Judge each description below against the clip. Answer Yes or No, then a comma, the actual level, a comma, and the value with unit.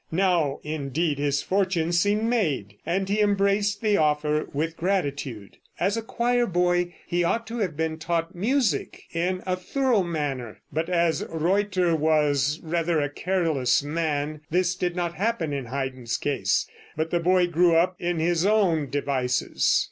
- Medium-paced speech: Yes, average, 155 wpm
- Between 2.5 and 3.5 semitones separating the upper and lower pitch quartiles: No, average, 3.9 semitones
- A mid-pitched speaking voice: Yes, medium, 170 Hz